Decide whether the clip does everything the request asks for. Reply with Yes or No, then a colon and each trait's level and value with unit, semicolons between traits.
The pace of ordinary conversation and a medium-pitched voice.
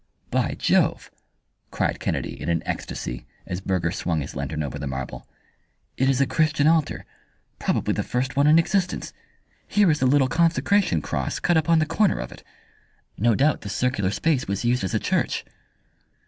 No: average, 175 wpm; low, 130 Hz